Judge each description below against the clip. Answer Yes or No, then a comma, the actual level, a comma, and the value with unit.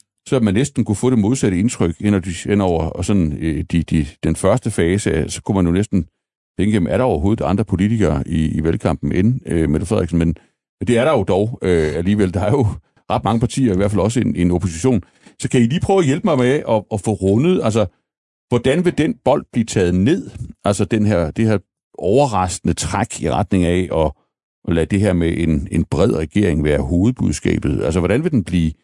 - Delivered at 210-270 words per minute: Yes, average, 220 wpm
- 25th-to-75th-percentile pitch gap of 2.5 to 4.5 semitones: No, average, 4.9 semitones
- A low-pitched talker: Yes, low, 100 Hz